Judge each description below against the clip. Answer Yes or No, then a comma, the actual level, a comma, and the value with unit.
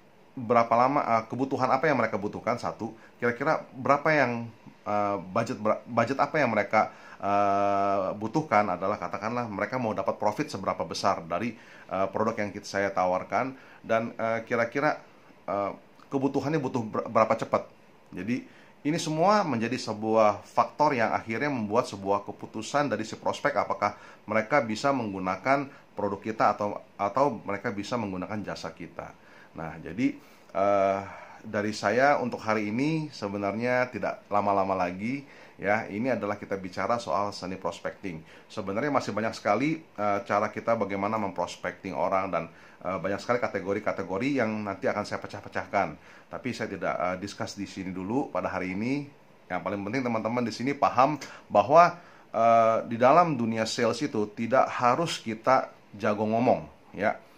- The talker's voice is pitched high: No, low, 110 Hz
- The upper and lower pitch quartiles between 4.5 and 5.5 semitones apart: No, average, 3.8 semitones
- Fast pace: Yes, fast, 145 wpm